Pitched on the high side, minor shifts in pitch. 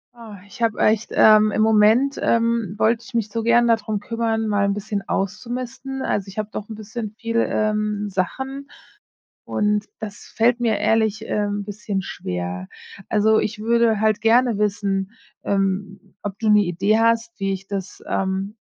Yes: high, 215 Hz; narrow, 2.2 semitones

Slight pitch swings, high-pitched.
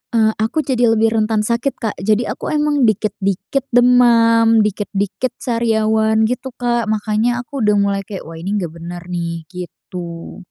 No: average, 3.3 semitones; high, 220 Hz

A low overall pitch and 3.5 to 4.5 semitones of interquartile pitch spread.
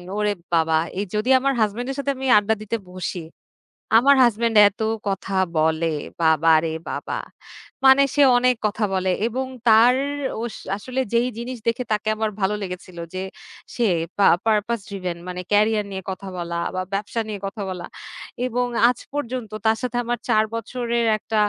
No: high, 215 Hz; average, 4.0 semitones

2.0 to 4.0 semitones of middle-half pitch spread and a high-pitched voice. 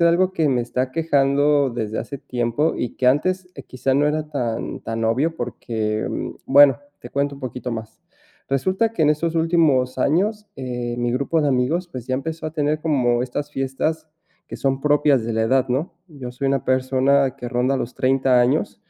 No: average, 3.5 semitones; low, 135 Hz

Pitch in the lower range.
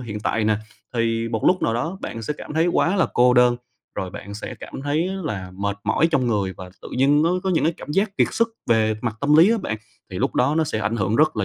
Yes: low, 120 Hz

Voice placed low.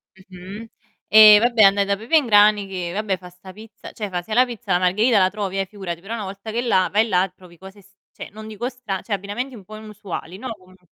No: high, 200 Hz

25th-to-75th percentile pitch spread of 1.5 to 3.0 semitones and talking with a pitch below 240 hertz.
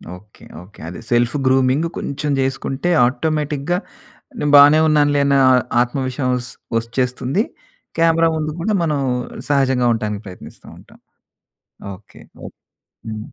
No: average, 3.7 semitones; low, 135 Hz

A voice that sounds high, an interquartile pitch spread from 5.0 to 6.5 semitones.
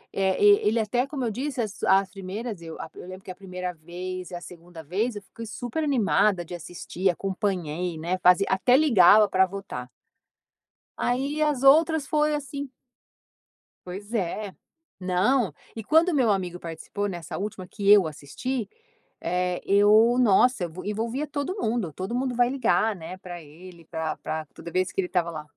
Yes: high, 195 Hz; wide, 5.4 semitones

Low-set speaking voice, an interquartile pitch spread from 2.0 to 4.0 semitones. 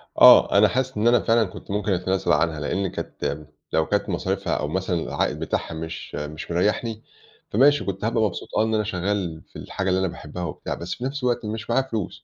No: low, 100 Hz; average, 4.4 semitones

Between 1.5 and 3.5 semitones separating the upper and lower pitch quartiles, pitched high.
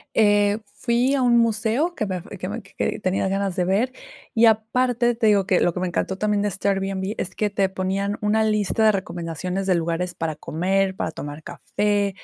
Yes: average, 2.7 semitones; high, 200 Hz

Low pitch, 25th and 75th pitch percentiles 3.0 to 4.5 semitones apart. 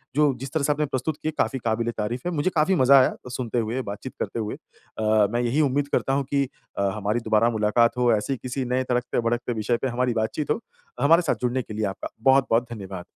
Yes: low, 125 Hz; average, 3.3 semitones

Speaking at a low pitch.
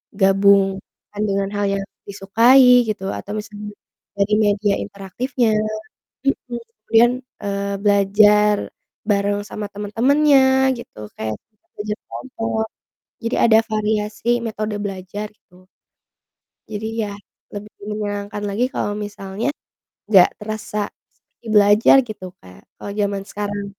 No: high, 210 Hz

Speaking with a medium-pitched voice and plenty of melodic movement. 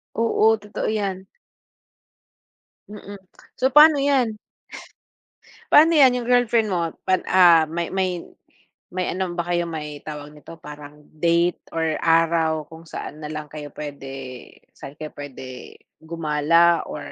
No: medium, 170 Hz; average, 4.8 semitones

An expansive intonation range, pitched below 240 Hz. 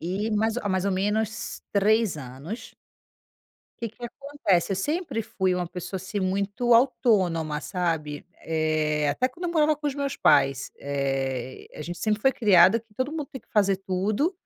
Yes: wide, 5.9 semitones; high, 200 Hz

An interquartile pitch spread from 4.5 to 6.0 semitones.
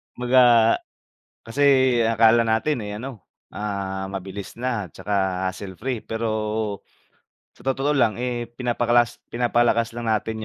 No: average, 2.7 semitones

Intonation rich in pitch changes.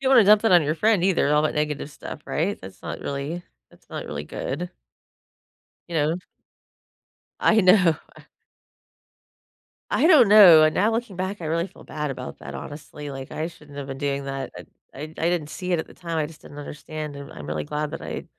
No: average, 4.1 semitones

